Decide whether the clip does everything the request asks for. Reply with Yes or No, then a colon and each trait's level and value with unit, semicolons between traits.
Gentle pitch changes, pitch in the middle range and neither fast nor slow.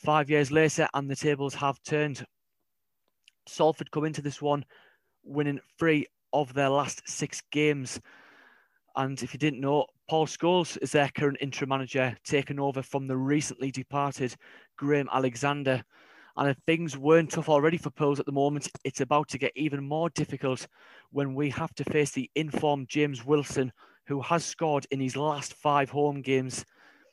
Yes: narrow, 1.9 semitones; medium, 145 Hz; average, 170 wpm